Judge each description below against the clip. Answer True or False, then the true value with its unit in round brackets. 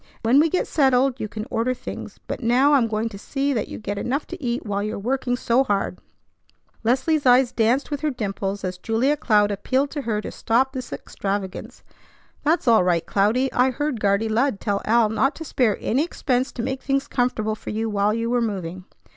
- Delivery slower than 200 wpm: False (205 wpm)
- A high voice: True (235 Hz)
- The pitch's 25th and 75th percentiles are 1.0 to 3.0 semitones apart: False (4.1 semitones)